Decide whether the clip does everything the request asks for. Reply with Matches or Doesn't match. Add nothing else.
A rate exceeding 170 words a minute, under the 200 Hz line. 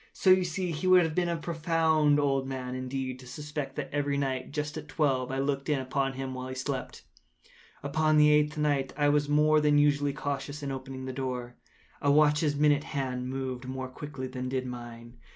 Matches